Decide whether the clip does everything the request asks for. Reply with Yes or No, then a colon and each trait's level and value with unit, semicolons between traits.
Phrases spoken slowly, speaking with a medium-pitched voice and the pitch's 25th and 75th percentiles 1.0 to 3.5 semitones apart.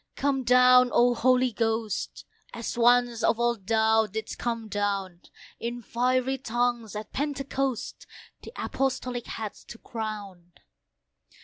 No: slow, 120 wpm; high, 235 Hz; narrow, 2.4 semitones